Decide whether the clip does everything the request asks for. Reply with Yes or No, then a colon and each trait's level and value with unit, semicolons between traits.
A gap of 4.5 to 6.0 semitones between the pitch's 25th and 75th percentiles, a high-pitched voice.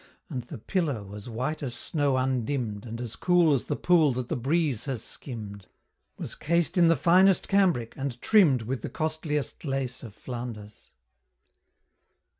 No: average, 5.2 semitones; low, 135 Hz